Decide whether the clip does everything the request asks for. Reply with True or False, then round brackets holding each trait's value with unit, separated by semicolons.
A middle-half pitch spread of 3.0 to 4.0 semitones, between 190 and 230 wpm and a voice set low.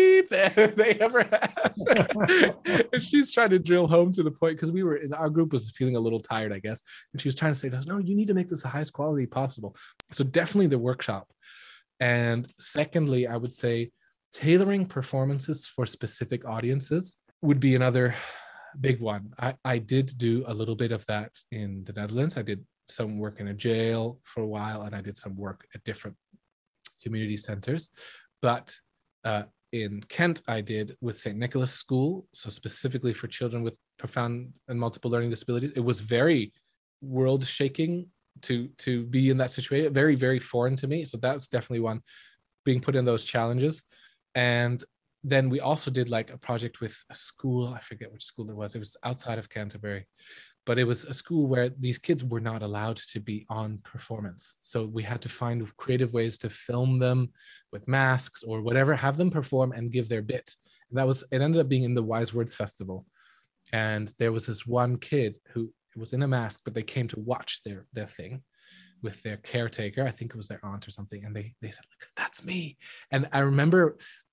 True (3.5 semitones; 200 wpm; 125 Hz)